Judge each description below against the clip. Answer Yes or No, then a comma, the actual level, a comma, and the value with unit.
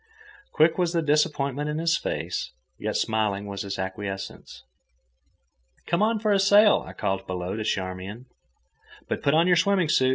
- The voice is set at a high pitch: No, medium, 140 Hz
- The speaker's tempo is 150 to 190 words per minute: Yes, average, 165 wpm